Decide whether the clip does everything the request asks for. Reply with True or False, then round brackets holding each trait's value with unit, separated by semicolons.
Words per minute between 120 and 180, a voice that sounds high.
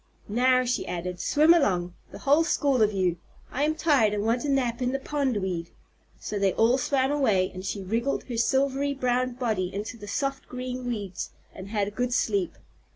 False (195 wpm; 245 Hz)